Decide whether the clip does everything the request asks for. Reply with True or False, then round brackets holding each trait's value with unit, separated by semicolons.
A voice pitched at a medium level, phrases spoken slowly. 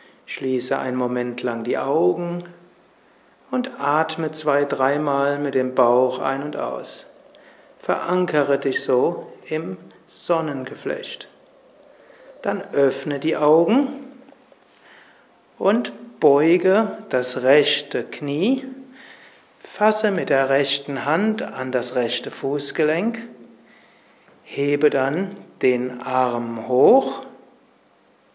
True (145 Hz; 95 wpm)